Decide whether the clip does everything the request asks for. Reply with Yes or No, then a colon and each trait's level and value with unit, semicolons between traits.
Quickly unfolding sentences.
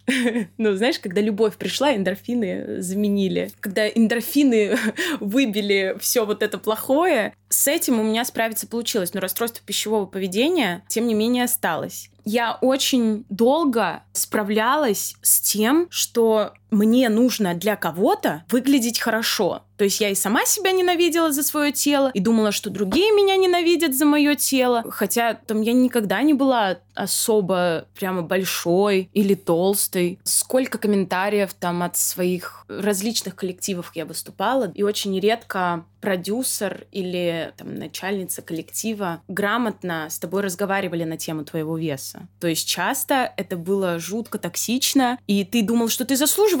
No: average, 140 wpm